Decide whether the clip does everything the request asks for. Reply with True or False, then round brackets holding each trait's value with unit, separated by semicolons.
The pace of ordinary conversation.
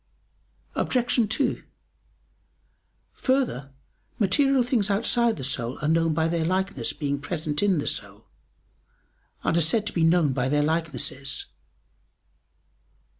False (125 wpm)